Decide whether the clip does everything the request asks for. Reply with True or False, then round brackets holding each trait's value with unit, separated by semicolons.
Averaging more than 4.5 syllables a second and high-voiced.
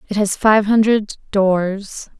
False (3.3 syllables/s; 205 Hz)